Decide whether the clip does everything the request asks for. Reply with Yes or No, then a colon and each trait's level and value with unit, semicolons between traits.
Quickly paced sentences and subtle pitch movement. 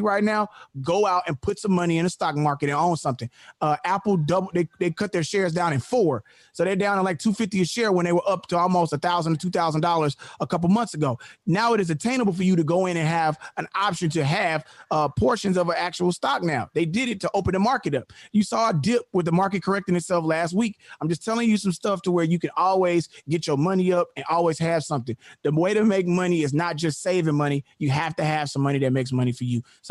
No: fast, 260 wpm; average, 3.7 semitones